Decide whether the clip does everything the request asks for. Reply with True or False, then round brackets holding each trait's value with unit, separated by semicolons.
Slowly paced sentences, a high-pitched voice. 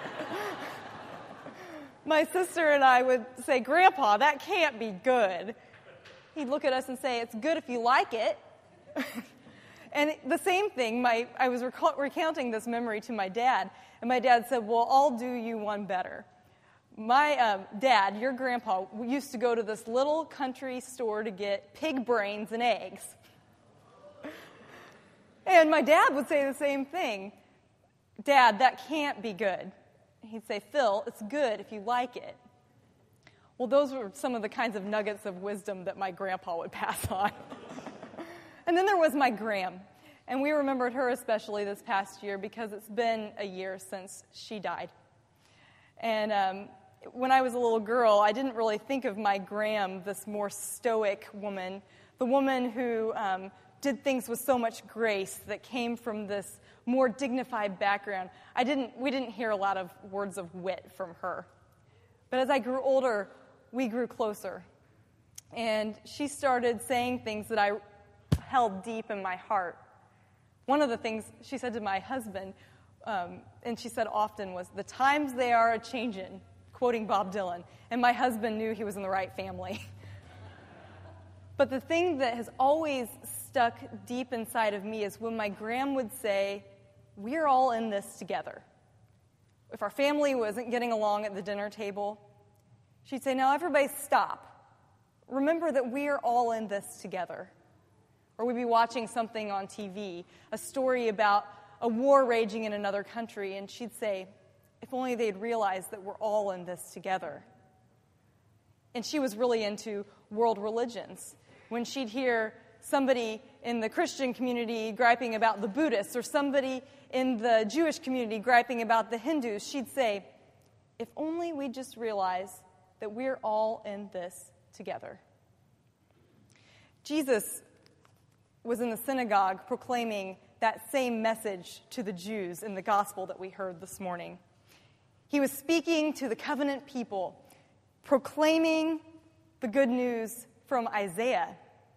False (160 wpm; 230 Hz)